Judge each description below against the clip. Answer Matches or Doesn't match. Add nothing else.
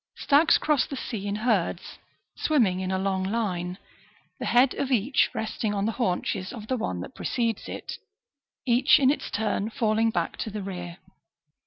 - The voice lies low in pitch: Doesn't match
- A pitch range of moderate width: Matches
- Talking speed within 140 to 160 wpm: Doesn't match